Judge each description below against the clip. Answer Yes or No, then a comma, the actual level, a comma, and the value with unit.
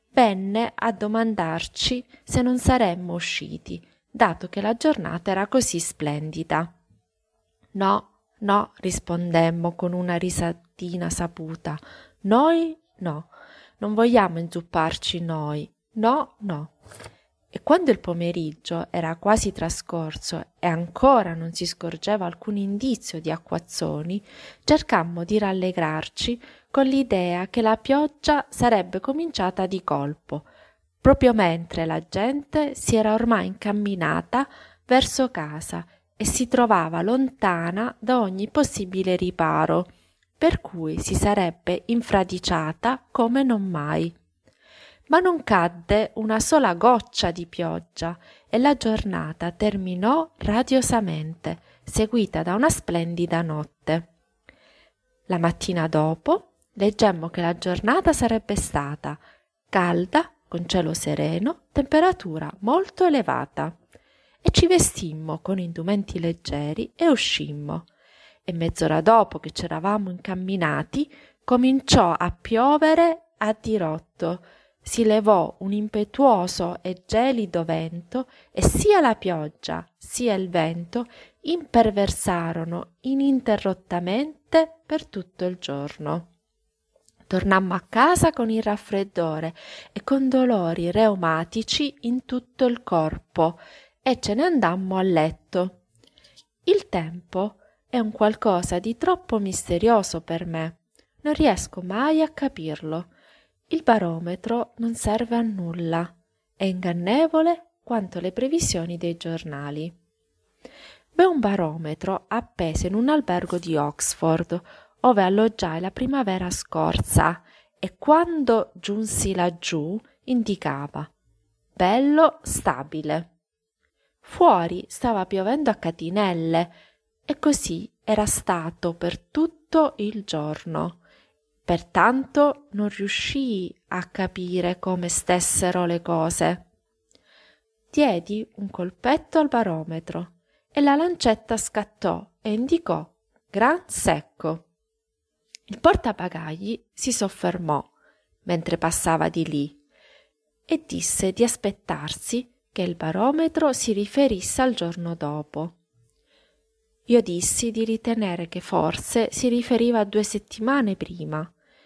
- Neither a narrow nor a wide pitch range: No, wide, 6.3 semitones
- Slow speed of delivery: Yes, slow, 110 wpm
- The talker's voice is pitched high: Yes, high, 195 Hz